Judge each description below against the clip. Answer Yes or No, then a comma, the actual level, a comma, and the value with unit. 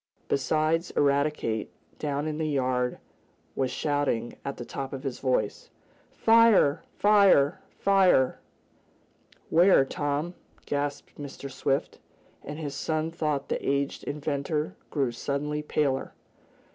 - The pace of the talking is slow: Yes, slow, 115 wpm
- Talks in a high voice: No, medium, 145 Hz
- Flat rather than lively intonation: Yes, narrow, 2.2 semitones